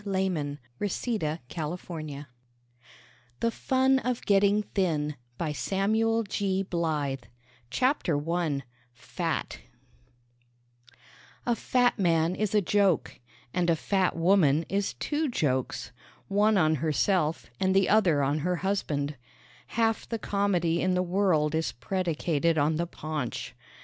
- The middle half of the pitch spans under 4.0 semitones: No, average, 4.8 semitones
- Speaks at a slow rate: Yes, slow, 110 wpm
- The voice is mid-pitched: Yes, medium, 175 Hz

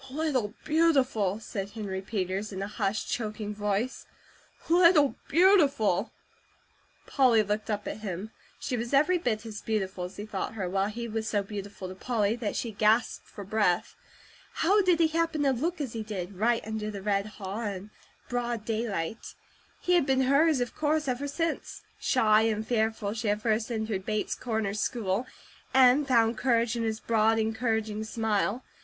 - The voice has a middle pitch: No, high, 220 Hz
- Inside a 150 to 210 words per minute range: Yes, average, 170 wpm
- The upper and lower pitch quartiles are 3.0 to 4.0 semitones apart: Yes, average, 3.6 semitones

